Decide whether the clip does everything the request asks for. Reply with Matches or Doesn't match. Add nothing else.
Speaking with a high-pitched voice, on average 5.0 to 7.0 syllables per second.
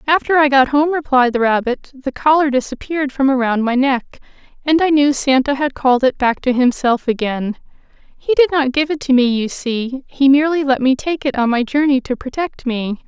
Matches